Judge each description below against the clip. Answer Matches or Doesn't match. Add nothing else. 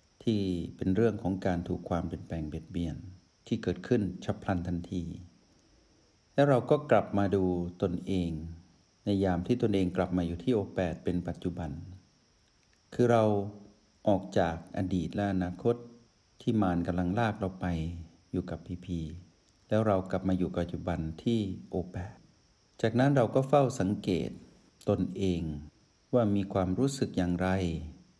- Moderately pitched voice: Doesn't match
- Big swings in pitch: Doesn't match